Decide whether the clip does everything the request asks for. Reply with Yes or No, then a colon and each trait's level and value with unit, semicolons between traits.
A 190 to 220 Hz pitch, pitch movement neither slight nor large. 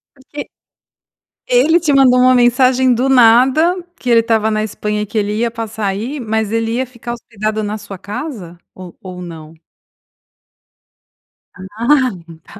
No: high, 230 Hz; average, 3.4 semitones